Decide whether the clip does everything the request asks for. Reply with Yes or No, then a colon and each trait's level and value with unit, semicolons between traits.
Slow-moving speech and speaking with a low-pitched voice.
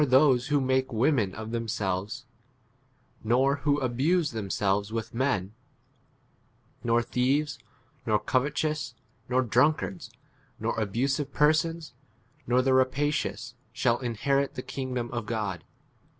Yes: slow, 130 wpm; low, 125 Hz